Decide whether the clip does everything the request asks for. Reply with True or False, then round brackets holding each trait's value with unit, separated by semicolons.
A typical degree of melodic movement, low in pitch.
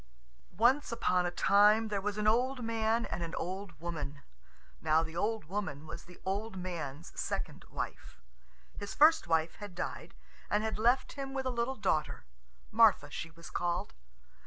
False (5.0 semitones; 200 Hz)